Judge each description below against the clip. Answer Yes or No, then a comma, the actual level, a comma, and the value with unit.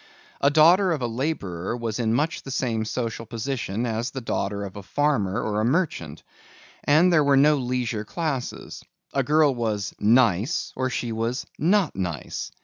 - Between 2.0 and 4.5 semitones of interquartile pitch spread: No, average, 5.0 semitones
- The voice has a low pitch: Yes, low, 125 Hz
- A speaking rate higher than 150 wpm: Yes, average, 170 wpm